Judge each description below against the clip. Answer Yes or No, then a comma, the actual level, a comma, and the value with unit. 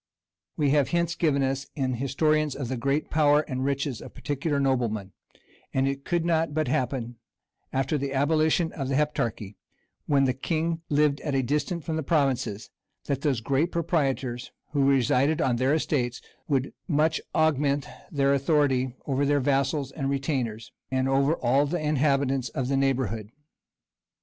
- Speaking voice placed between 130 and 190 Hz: Yes, medium, 140 Hz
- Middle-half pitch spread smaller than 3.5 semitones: Yes, narrow, 2.4 semitones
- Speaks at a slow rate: No, average, 160 wpm